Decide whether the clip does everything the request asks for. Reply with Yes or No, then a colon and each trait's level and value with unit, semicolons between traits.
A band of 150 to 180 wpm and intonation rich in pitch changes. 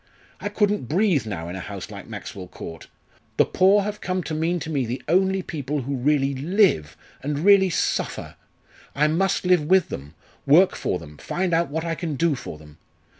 No: average, 195 wpm; wide, 6.4 semitones